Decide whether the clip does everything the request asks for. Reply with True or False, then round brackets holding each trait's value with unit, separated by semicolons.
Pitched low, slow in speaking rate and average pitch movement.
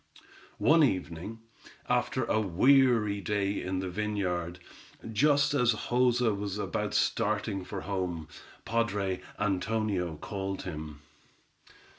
True (100 Hz; 105 wpm; 3.6 semitones)